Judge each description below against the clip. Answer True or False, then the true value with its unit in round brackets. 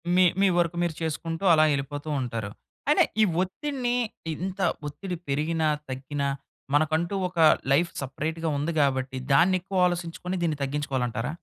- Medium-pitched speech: True (160 Hz)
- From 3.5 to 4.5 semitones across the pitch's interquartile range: True (4.2 semitones)